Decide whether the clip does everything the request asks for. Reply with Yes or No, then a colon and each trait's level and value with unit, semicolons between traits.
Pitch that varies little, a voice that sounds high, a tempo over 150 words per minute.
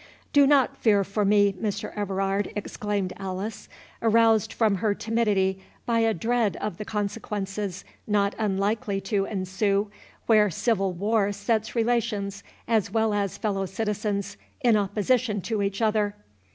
No: narrow, 2.0 semitones; high, 205 Hz; average, 140 wpm